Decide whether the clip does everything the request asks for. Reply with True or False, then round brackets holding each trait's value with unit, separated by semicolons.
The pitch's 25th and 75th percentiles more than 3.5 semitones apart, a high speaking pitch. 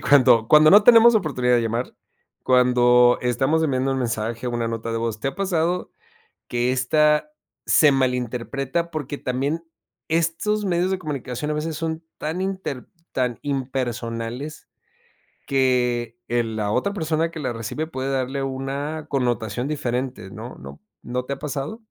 False (4.2 semitones; 135 Hz)